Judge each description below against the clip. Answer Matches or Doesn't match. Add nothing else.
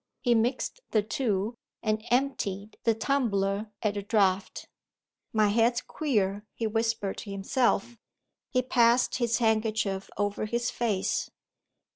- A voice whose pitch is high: Matches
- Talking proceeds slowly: Matches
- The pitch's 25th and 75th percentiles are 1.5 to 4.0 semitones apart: Matches